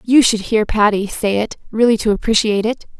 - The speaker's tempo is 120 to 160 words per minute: No, average, 200 wpm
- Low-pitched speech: No, high, 215 Hz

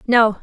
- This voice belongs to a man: No, female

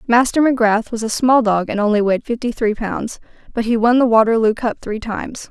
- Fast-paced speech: Yes, fast, 220 wpm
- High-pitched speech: Yes, high, 225 Hz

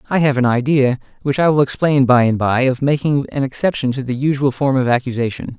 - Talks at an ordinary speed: No, fast, 225 wpm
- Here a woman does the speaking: No, male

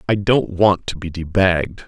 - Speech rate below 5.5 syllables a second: Yes, 4.9 syllables/s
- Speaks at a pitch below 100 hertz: Yes, very low, 90 Hz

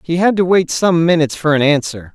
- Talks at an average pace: No, fast, 250 wpm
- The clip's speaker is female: No, male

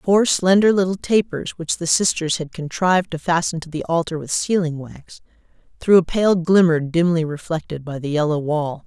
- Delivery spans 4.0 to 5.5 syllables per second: Yes, 5.0 syllables/s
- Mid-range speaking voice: Yes, medium, 165 Hz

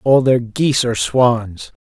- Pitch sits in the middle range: No, low, 130 Hz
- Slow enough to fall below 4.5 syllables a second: Yes, 4.2 syllables/s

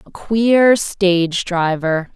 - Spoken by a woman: Yes, female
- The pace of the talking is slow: Yes, slow, 110 wpm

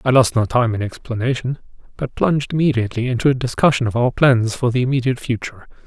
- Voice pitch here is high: No, low, 125 Hz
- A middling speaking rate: Yes, average, 195 wpm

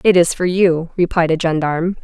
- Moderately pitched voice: Yes, medium, 170 Hz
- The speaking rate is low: No, fast, 205 wpm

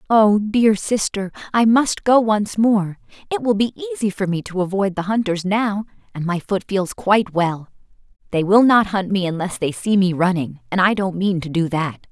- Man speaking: No, female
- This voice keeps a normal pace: No, fast, 210 wpm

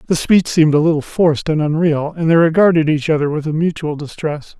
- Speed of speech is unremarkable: No, fast, 220 wpm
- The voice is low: No, medium, 155 Hz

